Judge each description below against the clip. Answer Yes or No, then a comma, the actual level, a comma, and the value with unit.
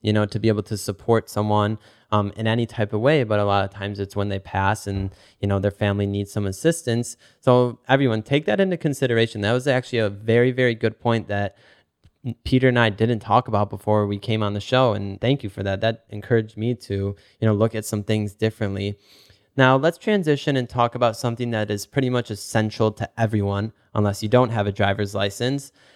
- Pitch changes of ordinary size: Yes, average, 3.1 semitones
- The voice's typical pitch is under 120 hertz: Yes, low, 110 Hz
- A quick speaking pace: Yes, fast, 220 wpm